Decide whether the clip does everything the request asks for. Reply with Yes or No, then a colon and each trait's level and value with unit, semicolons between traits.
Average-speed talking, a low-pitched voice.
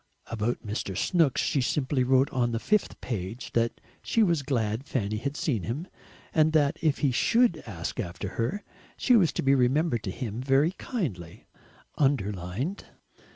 Yes: average, 160 wpm; low, 130 Hz